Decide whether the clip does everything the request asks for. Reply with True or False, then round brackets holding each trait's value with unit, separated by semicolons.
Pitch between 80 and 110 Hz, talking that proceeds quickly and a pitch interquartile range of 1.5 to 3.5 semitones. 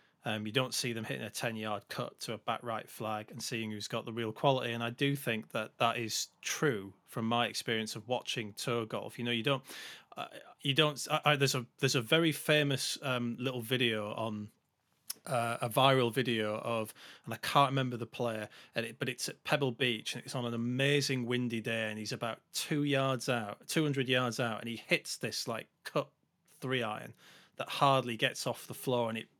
False (120 Hz; 215 wpm; 2.8 semitones)